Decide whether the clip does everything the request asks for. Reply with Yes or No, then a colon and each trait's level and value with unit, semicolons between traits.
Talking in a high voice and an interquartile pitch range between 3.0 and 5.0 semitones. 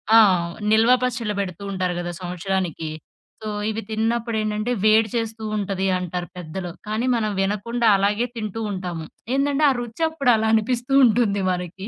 Yes: high, 215 Hz; average, 3.6 semitones